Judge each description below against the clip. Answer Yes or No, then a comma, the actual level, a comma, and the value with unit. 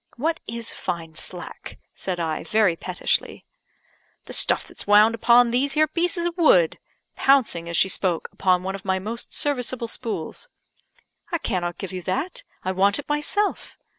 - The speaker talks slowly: No, average, 165 wpm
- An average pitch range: No, wide, 7.2 semitones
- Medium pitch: No, high, 215 Hz